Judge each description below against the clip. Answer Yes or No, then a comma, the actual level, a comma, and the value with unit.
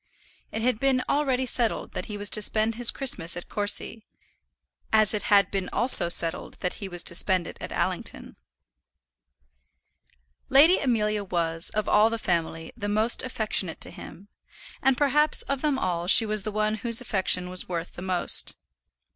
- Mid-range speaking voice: No, high, 210 Hz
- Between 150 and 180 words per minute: Yes, average, 170 wpm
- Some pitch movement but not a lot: Yes, average, 4.7 semitones